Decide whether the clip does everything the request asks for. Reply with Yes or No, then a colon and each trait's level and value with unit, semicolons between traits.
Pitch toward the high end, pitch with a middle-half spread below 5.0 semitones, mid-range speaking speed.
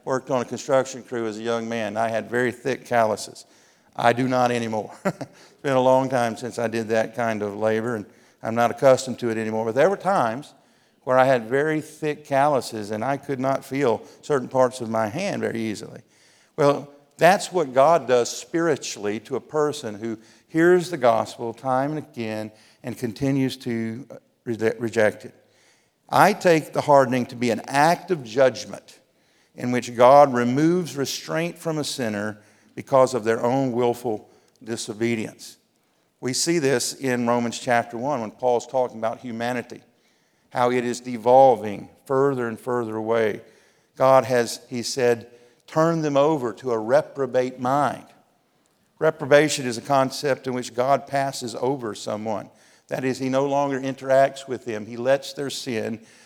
No: low, 125 Hz; average, 2.9 semitones; average, 170 wpm